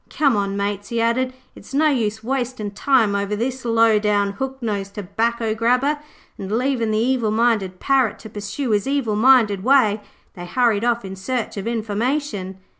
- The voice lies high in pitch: Yes, high, 225 Hz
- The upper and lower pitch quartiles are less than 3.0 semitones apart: No, average, 3.8 semitones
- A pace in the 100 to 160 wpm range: No, average, 175 wpm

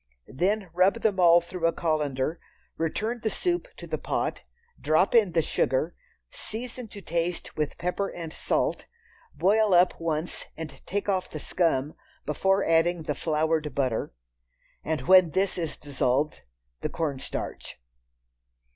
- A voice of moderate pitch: Yes, medium, 170 Hz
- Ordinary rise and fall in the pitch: Yes, average, 3.8 semitones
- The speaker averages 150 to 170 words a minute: No, average, 140 wpm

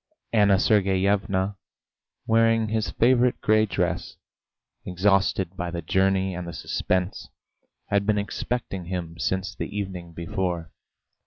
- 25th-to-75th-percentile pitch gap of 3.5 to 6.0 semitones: No, narrow, 2.6 semitones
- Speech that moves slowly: Yes, slow, 115 wpm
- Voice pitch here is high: No, very low, 95 Hz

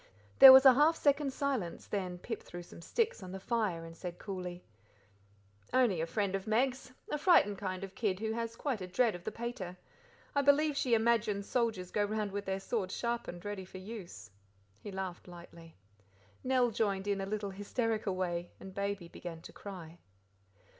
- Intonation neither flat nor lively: Yes, average, 4.4 semitones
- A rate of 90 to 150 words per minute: No, average, 190 wpm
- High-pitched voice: Yes, high, 200 Hz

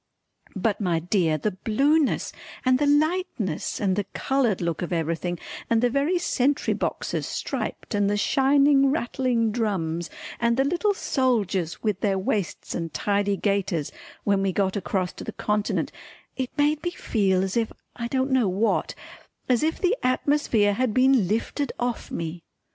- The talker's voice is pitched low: No, high, 220 Hz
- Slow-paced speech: No, average, 160 wpm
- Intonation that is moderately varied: No, wide, 5.9 semitones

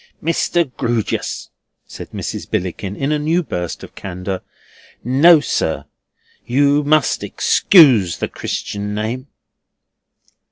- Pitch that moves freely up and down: Yes, wide, 6.8 semitones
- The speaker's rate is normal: No, slow, 110 wpm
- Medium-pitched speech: No, low, 130 Hz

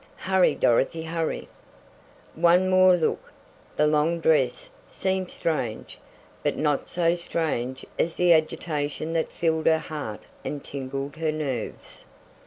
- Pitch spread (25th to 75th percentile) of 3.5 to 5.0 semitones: No, average, 2.8 semitones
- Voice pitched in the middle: Yes, medium, 160 Hz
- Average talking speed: No, slow, 125 wpm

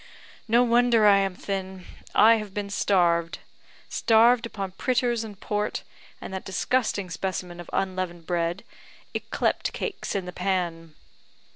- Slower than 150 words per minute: Yes, slow, 135 wpm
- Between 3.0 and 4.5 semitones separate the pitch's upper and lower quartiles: Yes, average, 3.7 semitones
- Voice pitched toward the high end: Yes, high, 195 Hz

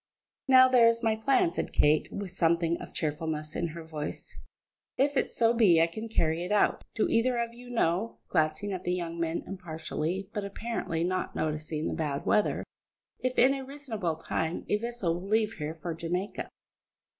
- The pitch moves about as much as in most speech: No, wide, 5.9 semitones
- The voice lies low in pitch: No, medium, 180 Hz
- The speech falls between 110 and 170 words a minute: No, average, 185 wpm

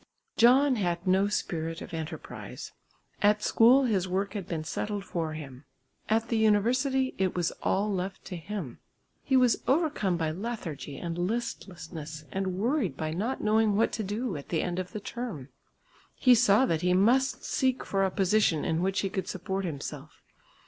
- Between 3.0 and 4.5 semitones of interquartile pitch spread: No, average, 5.0 semitones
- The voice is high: Yes, high, 195 Hz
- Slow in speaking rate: No, average, 175 wpm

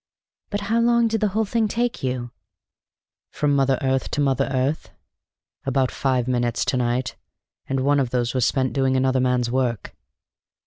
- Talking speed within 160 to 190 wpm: Yes, average, 175 wpm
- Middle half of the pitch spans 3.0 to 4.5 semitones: No, narrow, 2.6 semitones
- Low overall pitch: Yes, low, 130 Hz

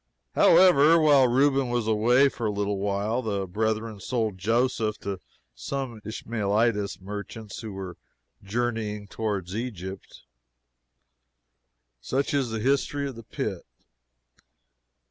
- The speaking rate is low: Yes, slow, 115 wpm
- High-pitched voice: No, low, 110 Hz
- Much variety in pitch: No, average, 3.7 semitones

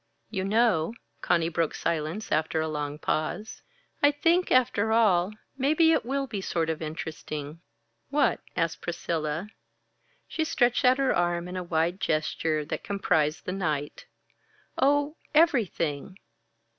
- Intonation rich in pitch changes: Yes, wide, 7.5 semitones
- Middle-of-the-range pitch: Yes, medium, 180 Hz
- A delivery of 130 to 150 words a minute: Yes, slow, 135 wpm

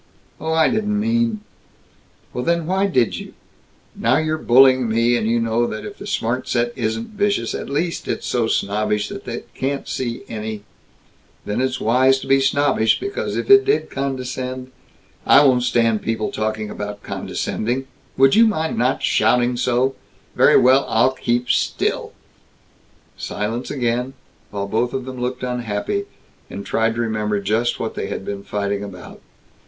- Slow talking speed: No, average, 170 wpm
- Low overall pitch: Yes, low, 125 Hz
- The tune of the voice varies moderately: Yes, average, 3.4 semitones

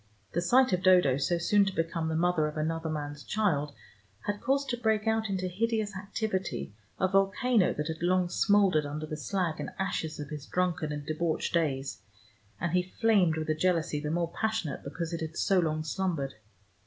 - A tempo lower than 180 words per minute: No, average, 190 wpm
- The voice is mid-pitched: Yes, medium, 175 Hz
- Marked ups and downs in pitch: No, average, 4.0 semitones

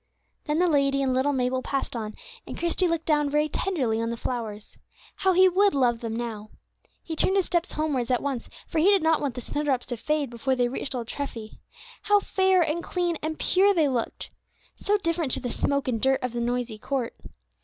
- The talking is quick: Yes, fast, 215 wpm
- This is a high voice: Yes, very high, 280 Hz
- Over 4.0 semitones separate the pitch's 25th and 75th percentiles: Yes, wide, 5.5 semitones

